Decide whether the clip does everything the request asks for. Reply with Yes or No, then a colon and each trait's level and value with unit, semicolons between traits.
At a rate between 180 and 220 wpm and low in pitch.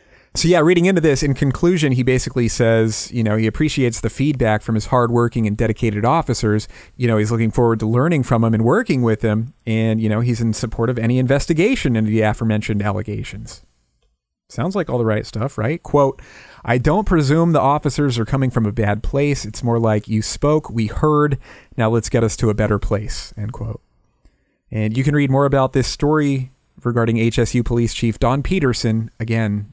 Yes: average, 200 wpm; low, 115 Hz